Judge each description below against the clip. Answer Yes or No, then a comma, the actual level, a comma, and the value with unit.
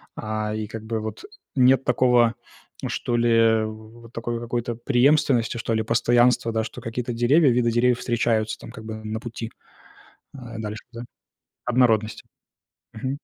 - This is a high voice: No, low, 115 Hz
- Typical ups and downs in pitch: No, narrow, 1.7 semitones